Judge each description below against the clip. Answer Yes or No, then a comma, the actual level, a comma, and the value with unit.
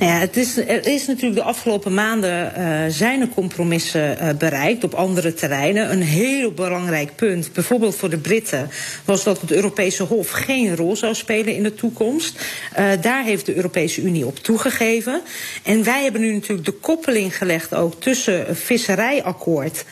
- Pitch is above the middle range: Yes, high, 200 Hz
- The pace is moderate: Yes, average, 175 wpm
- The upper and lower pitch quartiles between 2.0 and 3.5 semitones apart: No, average, 4.6 semitones